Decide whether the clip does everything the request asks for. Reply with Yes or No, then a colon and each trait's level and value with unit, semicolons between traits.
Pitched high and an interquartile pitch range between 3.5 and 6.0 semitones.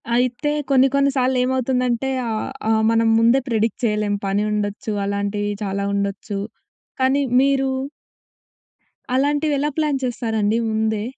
Yes: high, 230 Hz; average, 4.1 semitones